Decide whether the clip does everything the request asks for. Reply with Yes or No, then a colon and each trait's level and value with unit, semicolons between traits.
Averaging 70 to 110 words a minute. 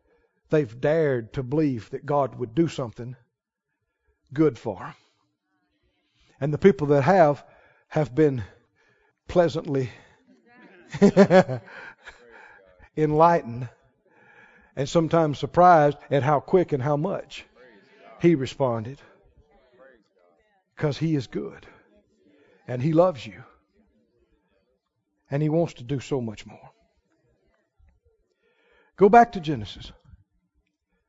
Yes: slow, 100 wpm